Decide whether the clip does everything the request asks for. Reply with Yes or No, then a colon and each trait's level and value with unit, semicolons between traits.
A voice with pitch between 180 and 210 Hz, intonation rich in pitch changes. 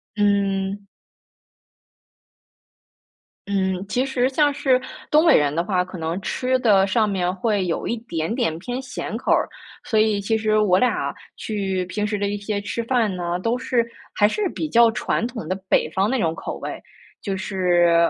No: high, 205 Hz; average, 4.1 semitones